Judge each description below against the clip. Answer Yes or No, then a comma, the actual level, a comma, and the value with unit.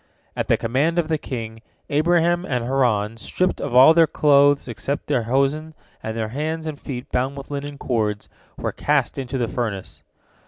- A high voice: No, low, 135 Hz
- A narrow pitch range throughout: No, average, 4.3 semitones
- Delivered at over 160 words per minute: Yes, average, 180 wpm